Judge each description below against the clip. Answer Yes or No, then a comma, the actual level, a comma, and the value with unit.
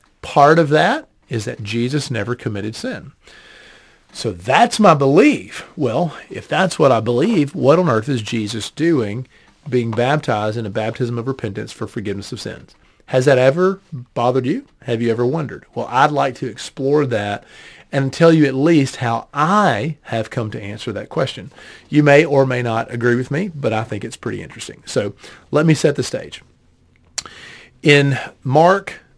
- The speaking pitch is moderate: No, low, 125 Hz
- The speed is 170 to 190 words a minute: Yes, average, 175 wpm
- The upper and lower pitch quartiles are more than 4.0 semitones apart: Yes, average, 4.4 semitones